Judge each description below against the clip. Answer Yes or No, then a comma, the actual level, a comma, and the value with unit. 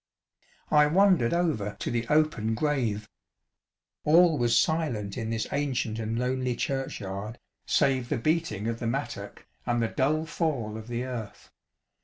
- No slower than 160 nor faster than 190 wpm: No, average, 145 wpm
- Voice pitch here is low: Yes, low, 120 Hz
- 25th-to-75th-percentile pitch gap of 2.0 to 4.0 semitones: No, average, 5.1 semitones